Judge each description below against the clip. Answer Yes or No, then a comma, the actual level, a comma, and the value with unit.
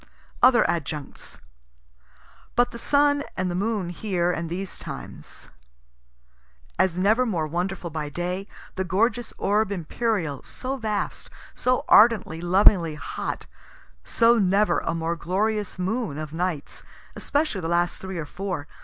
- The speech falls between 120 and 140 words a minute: Yes, slow, 135 wpm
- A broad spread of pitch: No, average, 4.4 semitones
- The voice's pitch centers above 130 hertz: Yes, high, 190 Hz